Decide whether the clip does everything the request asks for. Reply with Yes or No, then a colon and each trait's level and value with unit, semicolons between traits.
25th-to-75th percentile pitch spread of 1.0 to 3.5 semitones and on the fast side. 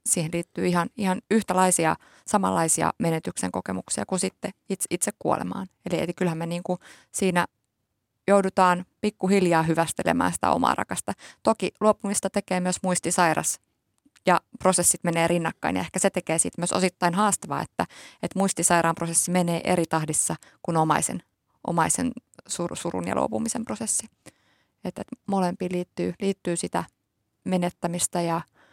No: narrow, 2.4 semitones; average, 135 wpm